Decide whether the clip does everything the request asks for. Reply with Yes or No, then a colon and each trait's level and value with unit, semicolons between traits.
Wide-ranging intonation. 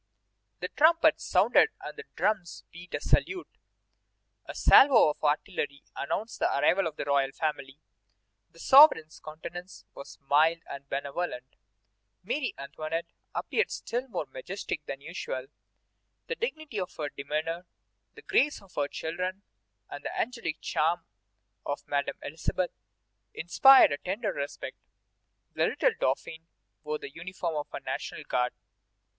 Yes: wide, 5.7 semitones